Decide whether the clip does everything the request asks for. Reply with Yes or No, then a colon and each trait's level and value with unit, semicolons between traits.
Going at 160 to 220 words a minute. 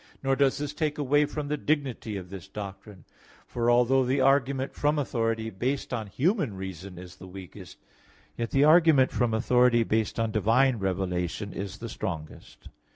Yes: average, 165 wpm